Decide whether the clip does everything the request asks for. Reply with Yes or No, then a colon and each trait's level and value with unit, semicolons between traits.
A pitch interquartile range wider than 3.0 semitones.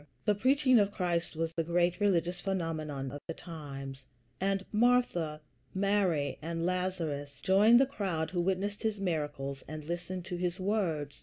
Yes: average, 4.0 semitones